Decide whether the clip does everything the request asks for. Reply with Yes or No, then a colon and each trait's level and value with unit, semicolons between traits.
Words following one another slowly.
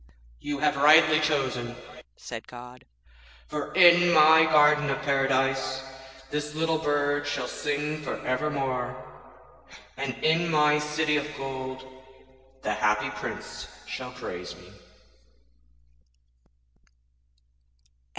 Yes: slow, 100 wpm